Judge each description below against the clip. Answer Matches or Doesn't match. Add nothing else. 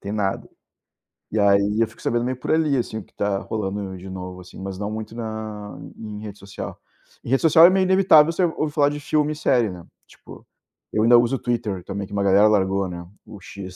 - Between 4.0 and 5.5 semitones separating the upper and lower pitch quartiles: Matches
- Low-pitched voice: Matches